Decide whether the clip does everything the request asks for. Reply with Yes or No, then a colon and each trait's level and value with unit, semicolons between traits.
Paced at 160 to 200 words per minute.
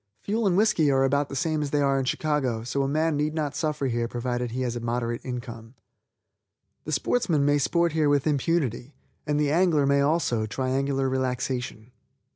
Yes: average, 190 wpm